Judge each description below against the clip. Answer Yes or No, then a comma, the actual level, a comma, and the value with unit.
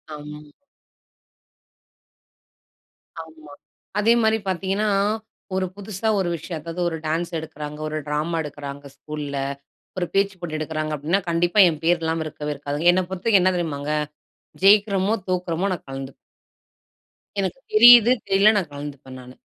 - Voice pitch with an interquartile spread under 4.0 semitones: No, average, 4.4 semitones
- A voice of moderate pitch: Yes, medium, 165 Hz